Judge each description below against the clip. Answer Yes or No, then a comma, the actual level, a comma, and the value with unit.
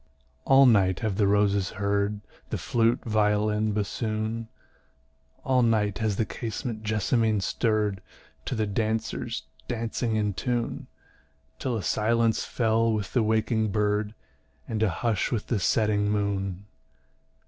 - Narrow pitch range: Yes, narrow, 1.8 semitones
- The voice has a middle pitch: No, low, 110 Hz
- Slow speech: Yes, slow, 130 wpm